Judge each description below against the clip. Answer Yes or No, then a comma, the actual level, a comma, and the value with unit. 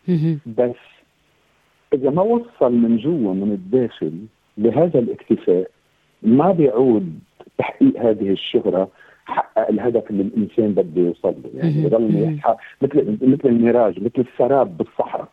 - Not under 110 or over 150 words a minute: Yes, average, 115 wpm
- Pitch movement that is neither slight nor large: No, wide, 6.5 semitones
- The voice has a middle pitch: No, low, 120 Hz